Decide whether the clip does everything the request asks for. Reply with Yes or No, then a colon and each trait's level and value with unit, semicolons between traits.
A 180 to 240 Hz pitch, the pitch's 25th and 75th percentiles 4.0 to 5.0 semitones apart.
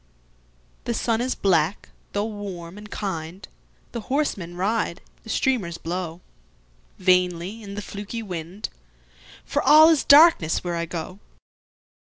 Yes: medium, 185 Hz; average, 4.4 semitones